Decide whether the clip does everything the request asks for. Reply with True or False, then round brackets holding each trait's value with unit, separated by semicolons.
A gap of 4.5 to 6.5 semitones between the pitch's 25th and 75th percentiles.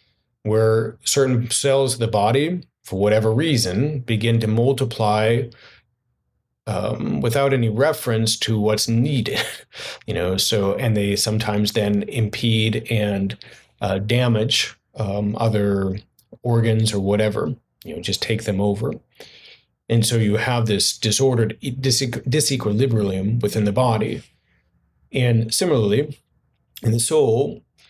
False (2.7 semitones)